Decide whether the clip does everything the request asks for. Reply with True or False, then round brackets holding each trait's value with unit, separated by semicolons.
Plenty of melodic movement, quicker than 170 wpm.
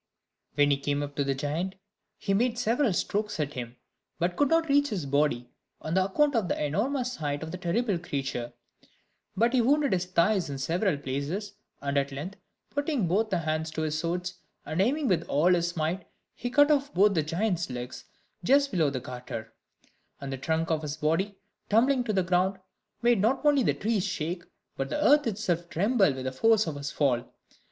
True (7.3 semitones; 195 wpm)